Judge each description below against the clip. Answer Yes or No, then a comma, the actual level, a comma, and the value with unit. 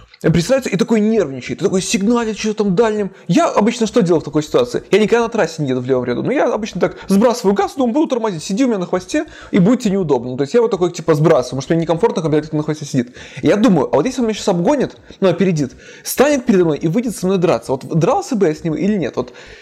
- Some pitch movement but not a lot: No, wide, 6.3 semitones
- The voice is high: Yes, high, 195 Hz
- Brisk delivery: Yes, fast, 270 wpm